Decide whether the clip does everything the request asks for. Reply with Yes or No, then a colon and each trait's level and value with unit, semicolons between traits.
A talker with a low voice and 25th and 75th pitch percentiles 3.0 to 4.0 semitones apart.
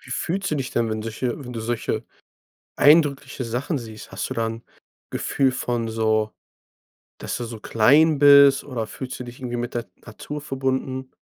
Yes: low, 125 Hz; average, 3.3 semitones